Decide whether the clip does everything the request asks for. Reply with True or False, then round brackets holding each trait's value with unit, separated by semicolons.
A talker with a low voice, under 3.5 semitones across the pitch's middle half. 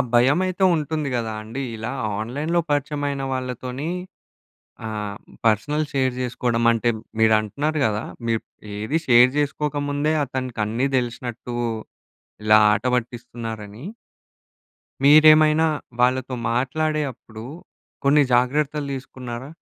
False (130 Hz; 4.1 semitones)